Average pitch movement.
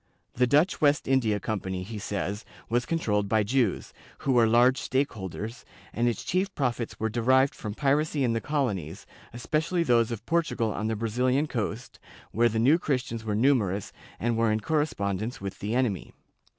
Yes: average, 3.9 semitones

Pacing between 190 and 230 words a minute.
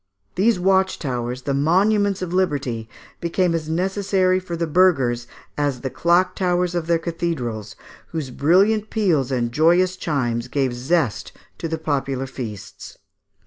No: average, 145 wpm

